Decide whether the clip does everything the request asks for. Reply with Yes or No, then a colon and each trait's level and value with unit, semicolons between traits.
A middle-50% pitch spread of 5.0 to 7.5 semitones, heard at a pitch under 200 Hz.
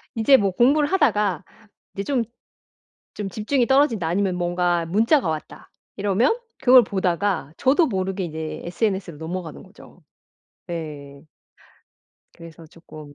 Yes: wide, 5.5 semitones; high, 190 Hz